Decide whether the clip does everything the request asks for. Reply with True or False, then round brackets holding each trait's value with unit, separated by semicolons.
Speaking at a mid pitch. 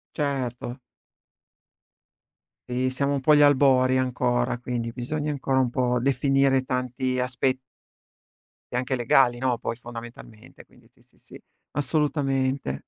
False (130 Hz)